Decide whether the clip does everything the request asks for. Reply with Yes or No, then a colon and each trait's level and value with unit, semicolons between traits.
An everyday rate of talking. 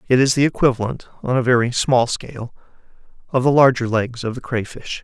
Yes: average, 190 wpm